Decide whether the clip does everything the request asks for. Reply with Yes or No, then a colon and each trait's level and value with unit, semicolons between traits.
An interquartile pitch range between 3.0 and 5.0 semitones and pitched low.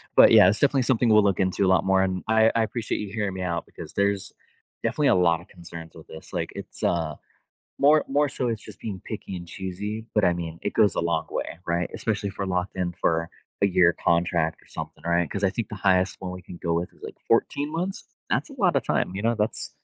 Yes: average, 4.1 semitones; very low, 95 Hz